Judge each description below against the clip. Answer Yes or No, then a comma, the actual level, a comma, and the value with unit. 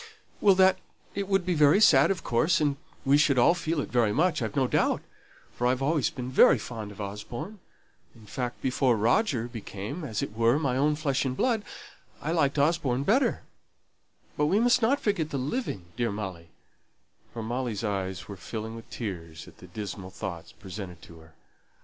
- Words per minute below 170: No, average, 185 wpm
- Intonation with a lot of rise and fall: Yes, wide, 6.9 semitones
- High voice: No, low, 125 Hz